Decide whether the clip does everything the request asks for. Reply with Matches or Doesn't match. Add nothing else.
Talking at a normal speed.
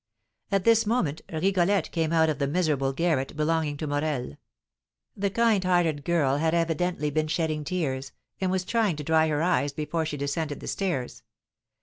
Matches